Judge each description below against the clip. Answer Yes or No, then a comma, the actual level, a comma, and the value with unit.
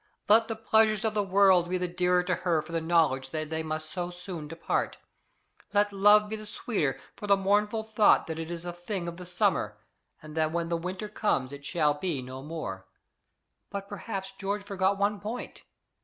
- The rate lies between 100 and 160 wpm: No, average, 200 wpm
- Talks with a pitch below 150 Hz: No, medium, 180 Hz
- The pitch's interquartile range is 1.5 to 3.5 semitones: No, average, 4.2 semitones